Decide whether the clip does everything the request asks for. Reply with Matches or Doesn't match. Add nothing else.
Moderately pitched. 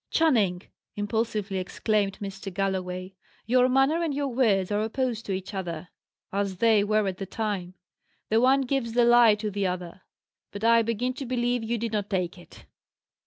Doesn't match